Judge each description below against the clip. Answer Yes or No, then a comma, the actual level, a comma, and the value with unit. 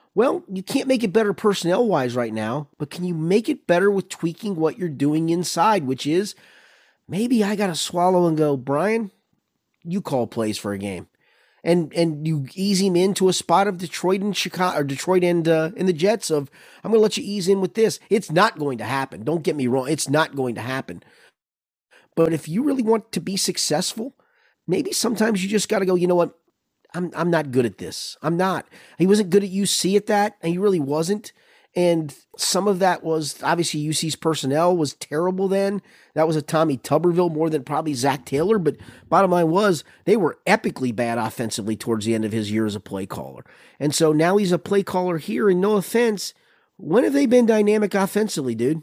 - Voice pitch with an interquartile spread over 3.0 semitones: Yes, average, 5.3 semitones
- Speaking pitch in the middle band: Yes, medium, 175 Hz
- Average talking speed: No, fast, 210 wpm